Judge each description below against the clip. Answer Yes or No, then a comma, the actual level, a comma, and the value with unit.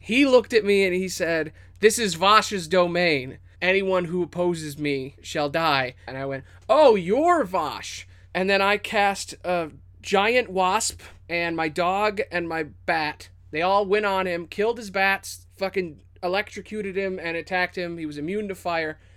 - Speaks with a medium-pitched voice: Yes, medium, 175 Hz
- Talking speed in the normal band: Yes, average, 170 wpm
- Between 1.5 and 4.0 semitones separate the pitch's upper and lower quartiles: No, average, 5.1 semitones